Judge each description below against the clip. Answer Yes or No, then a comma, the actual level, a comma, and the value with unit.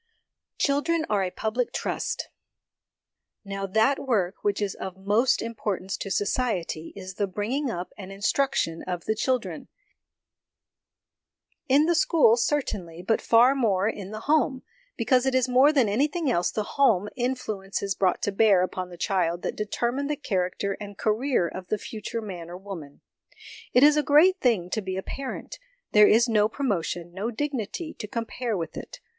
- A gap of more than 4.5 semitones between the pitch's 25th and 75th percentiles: Yes, average, 5.1 semitones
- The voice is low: No, high, 215 Hz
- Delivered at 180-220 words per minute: No, average, 170 wpm